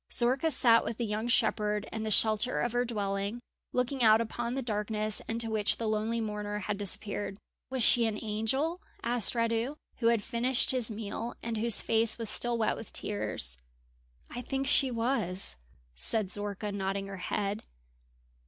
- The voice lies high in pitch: Yes, high, 225 Hz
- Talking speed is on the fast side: No, average, 170 wpm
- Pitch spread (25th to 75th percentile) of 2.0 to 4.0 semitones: Yes, narrow, 2.4 semitones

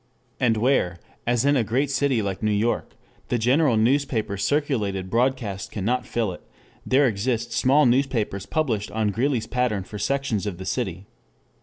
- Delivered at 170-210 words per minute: No, average, 160 wpm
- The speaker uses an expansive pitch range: No, average, 4.3 semitones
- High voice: No, low, 115 Hz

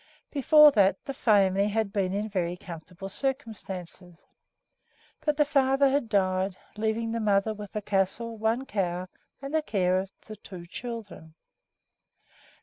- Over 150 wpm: No, average, 145 wpm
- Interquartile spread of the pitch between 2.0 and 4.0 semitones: Yes, average, 3.7 semitones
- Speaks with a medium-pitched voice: No, high, 205 Hz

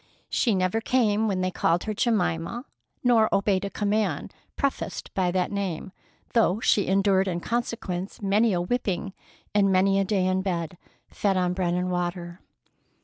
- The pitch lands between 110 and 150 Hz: No, high, 195 Hz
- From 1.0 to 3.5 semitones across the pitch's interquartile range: Yes, average, 2.8 semitones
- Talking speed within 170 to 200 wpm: No, average, 160 wpm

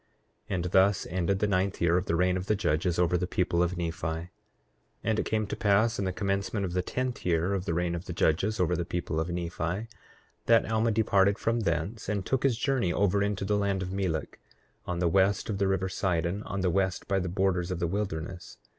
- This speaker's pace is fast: Yes, fast, 235 wpm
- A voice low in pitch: Yes, very low, 95 Hz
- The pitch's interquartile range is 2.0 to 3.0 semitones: Yes, narrow, 2.6 semitones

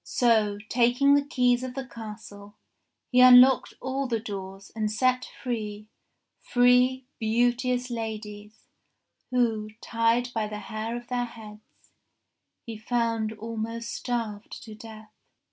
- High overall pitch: Yes, high, 230 Hz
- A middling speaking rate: No, slow, 125 wpm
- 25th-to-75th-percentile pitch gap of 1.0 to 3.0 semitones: Yes, narrow, 2.5 semitones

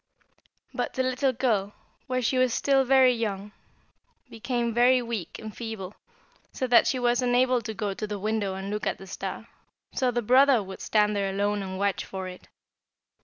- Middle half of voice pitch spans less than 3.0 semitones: No, average, 3.8 semitones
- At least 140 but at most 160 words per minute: No, average, 185 wpm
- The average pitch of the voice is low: No, high, 225 Hz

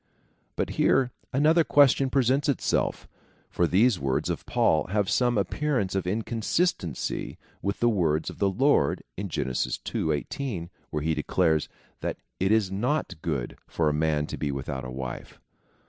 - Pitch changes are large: Yes, wide, 8.3 semitones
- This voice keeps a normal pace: Yes, average, 160 wpm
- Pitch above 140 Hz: No, very low, 95 Hz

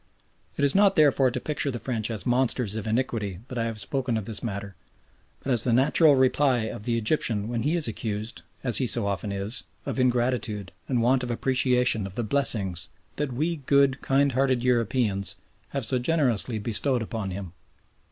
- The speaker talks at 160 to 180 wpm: No, average, 190 wpm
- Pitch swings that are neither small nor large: Yes, average, 3.6 semitones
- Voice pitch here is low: Yes, low, 120 Hz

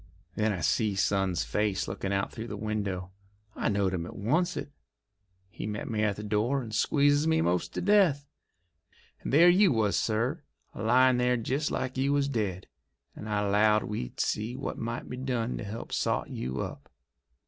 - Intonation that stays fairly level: No, average, 4.8 semitones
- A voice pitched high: No, low, 110 Hz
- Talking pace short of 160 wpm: No, average, 185 wpm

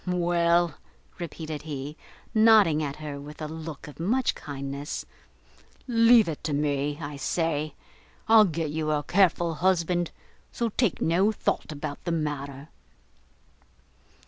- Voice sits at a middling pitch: Yes, medium, 160 Hz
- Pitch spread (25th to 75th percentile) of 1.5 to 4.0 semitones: Yes, average, 3.3 semitones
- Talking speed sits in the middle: No, slow, 130 wpm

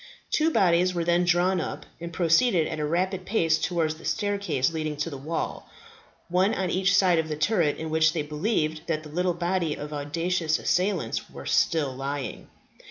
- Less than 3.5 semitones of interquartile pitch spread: Yes, average, 2.9 semitones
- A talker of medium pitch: Yes, medium, 170 Hz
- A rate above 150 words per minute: Yes, average, 185 wpm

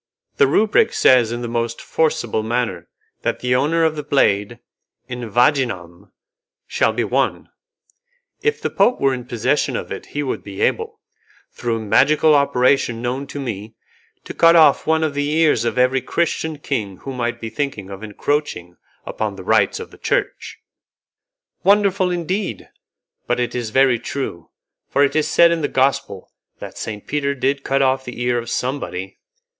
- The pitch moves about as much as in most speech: Yes, average, 4.2 semitones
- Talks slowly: No, average, 170 wpm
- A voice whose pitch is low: Yes, low, 130 Hz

